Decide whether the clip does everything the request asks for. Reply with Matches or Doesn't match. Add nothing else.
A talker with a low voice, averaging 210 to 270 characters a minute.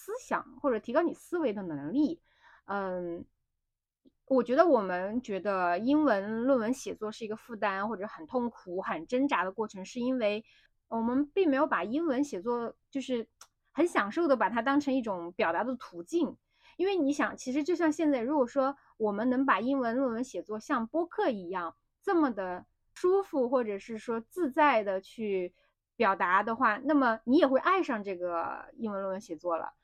Doesn't match